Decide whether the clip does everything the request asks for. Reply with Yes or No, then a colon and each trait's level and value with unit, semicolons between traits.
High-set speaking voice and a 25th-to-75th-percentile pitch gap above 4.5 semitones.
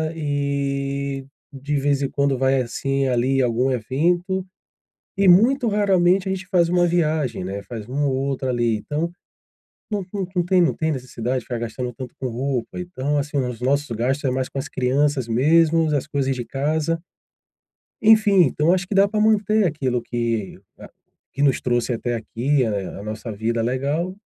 No: medium, 140 Hz; average, 5.2 semitones